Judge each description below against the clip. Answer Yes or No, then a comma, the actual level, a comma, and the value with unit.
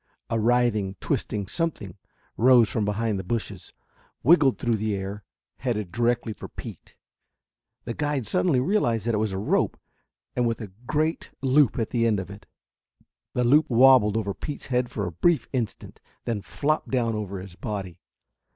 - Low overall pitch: Yes, low, 115 Hz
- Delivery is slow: No, average, 165 wpm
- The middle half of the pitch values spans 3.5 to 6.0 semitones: Yes, average, 3.8 semitones